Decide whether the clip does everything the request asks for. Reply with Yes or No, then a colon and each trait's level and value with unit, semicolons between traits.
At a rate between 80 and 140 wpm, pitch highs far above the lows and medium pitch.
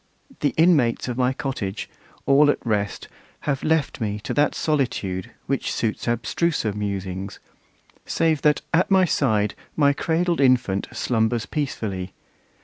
No: slow, 135 wpm; wide, 6.3 semitones; low, 125 Hz